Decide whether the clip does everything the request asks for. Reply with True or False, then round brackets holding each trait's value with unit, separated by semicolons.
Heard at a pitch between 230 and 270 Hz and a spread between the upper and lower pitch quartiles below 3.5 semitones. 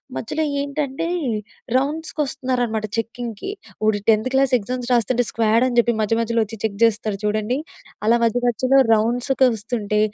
True (235 Hz; 2.9 semitones)